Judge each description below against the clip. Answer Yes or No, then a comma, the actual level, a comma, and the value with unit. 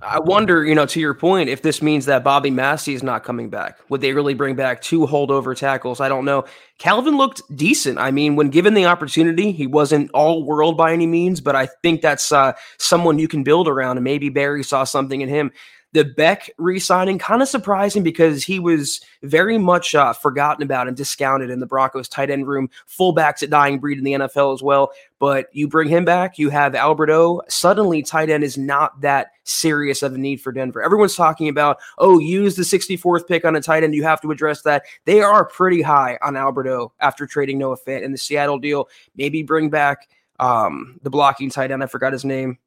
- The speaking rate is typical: No, fast, 220 wpm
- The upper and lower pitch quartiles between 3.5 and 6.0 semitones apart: No, average, 3.1 semitones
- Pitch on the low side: No, medium, 145 Hz